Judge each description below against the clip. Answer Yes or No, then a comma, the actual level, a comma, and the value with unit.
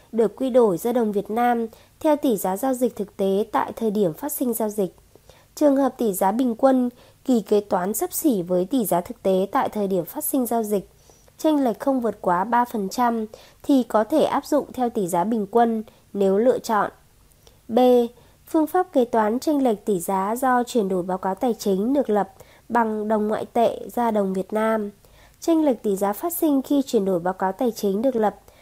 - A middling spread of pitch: Yes, average, 4.4 semitones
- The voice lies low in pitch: No, high, 230 Hz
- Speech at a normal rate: Yes, average, 220 wpm